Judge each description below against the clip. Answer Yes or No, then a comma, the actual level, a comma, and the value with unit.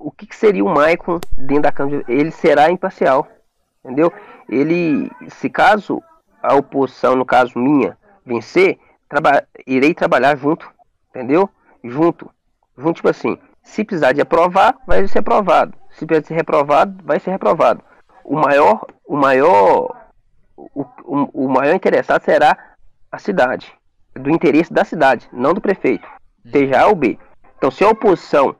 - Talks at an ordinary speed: Yes, average, 150 wpm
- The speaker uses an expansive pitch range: Yes, wide, 6.7 semitones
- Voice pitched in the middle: Yes, medium, 165 Hz